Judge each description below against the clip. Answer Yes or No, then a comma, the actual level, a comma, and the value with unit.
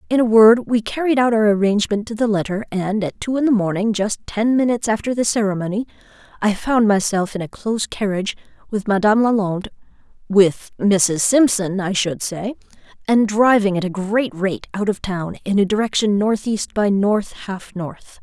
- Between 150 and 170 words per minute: No, average, 180 wpm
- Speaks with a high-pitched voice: Yes, high, 210 Hz